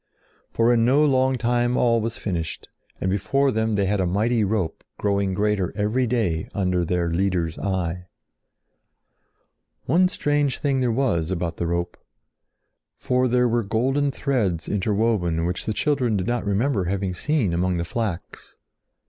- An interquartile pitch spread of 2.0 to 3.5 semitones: No, average, 5.3 semitones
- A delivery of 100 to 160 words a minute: Yes, average, 155 wpm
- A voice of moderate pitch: No, low, 105 Hz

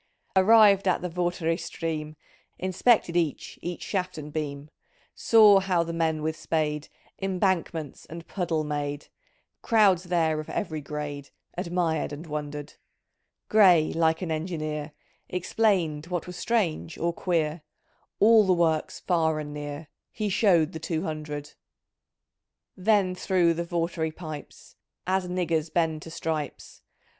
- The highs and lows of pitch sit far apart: No, average, 2.9 semitones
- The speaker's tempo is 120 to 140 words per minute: Yes, slow, 135 wpm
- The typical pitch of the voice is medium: Yes, medium, 165 Hz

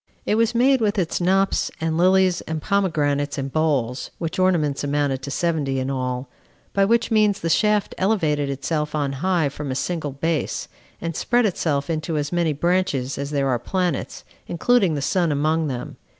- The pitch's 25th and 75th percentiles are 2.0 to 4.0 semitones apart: No, average, 4.7 semitones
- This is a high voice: No, medium, 160 Hz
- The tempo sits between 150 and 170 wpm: No, average, 180 wpm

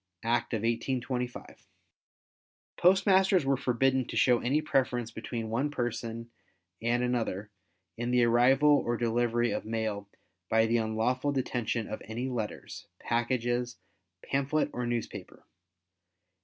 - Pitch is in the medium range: No, low, 120 Hz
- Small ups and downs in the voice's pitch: Yes, narrow, 2.2 semitones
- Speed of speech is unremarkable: No, slow, 120 wpm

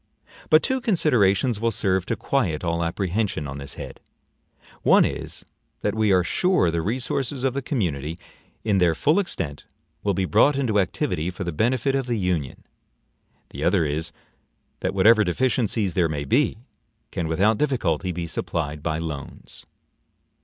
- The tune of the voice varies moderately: No, wide, 6.7 semitones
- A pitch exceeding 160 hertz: No, very low, 95 Hz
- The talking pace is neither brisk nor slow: Yes, average, 160 wpm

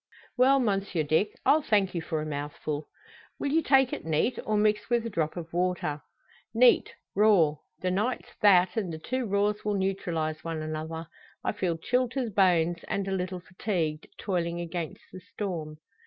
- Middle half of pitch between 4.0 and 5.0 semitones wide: Yes, average, 4.6 semitones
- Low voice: No, medium, 185 Hz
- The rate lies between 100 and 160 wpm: No, average, 180 wpm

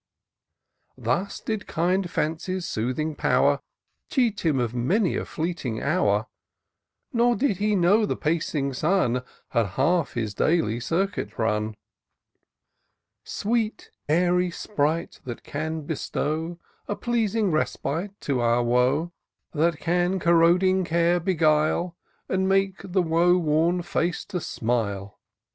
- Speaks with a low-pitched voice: No, medium, 170 Hz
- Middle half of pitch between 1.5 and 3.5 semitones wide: No, average, 5.0 semitones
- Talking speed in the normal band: No, slow, 120 wpm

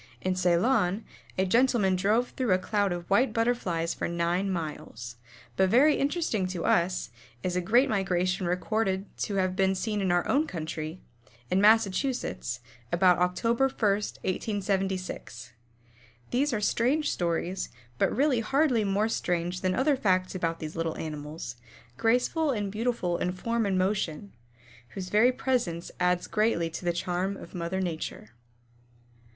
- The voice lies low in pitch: No, high, 190 Hz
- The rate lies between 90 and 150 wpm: Yes, average, 145 wpm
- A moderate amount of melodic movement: Yes, average, 4.3 semitones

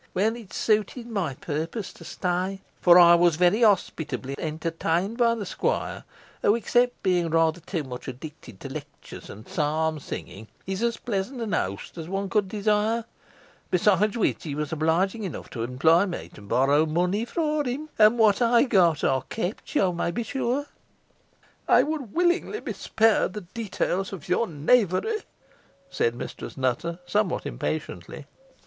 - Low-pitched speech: No, high, 190 Hz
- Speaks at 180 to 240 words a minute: No, average, 160 wpm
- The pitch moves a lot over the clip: Yes, wide, 5.9 semitones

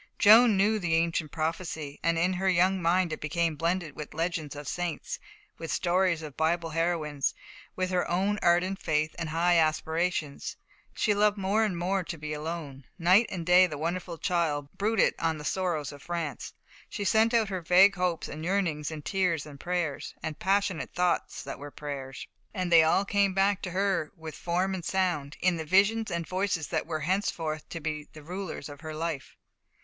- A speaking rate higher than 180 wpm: Yes, average, 190 wpm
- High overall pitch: No, medium, 170 Hz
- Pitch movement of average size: Yes, average, 3.1 semitones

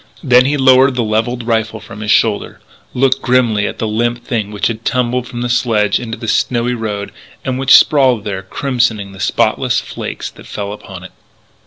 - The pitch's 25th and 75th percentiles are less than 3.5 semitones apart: Yes, average, 2.9 semitones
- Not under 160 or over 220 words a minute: Yes, average, 190 wpm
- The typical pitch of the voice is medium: No, low, 115 Hz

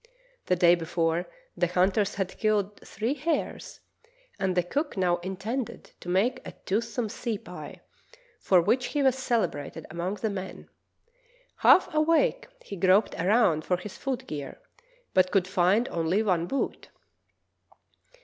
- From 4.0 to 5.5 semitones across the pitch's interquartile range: Yes, average, 4.8 semitones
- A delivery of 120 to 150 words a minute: Yes, average, 140 wpm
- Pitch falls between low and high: No, high, 195 Hz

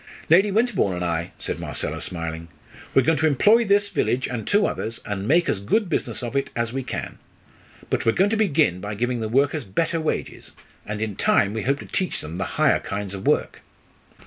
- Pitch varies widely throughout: Yes, wide, 8.9 semitones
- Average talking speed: No, fast, 210 wpm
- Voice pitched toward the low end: Yes, low, 120 Hz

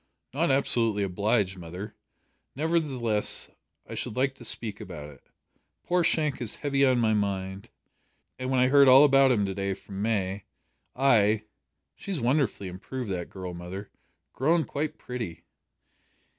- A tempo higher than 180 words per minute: No, average, 145 wpm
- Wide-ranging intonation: Yes, wide, 5.8 semitones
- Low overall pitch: Yes, low, 115 Hz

